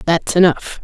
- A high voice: No, medium, 170 Hz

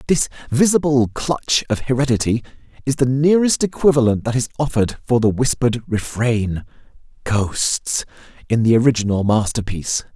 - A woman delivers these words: No, male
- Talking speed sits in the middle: No, slow, 125 wpm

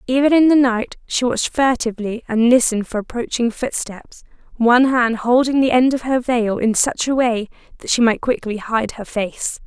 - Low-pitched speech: No, high, 240 Hz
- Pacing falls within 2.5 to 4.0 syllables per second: No, 5.1 syllables/s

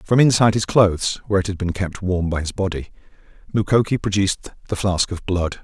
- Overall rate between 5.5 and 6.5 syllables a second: Yes, 6.0 syllables/s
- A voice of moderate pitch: No, very low, 95 Hz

